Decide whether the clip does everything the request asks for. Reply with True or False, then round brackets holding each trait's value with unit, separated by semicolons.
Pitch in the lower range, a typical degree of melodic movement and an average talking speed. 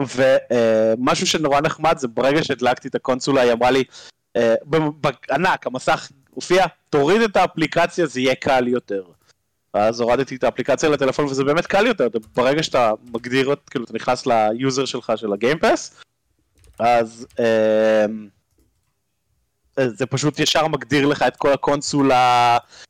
True (130 Hz; 3.9 semitones; 135 wpm)